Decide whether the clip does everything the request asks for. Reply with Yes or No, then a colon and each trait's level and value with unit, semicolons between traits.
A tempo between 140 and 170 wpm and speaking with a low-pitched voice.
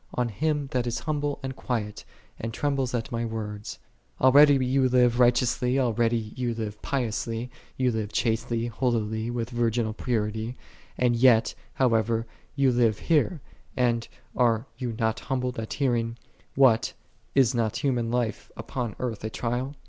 Yes: average, 155 wpm; low, 120 Hz